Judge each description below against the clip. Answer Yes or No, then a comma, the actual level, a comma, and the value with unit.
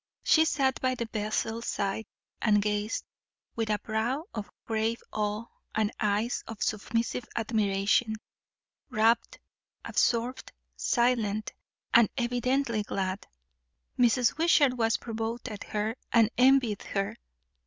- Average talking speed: No, slow, 115 wpm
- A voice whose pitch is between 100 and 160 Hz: No, high, 225 Hz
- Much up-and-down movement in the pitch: No, narrow, 2.4 semitones